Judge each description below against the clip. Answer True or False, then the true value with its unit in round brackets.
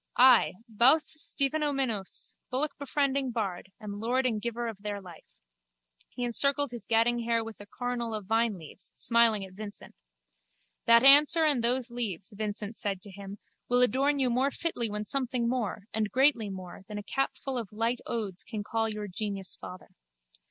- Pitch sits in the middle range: False (230 Hz)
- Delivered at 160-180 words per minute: True (165 wpm)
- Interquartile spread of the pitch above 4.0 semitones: False (3.7 semitones)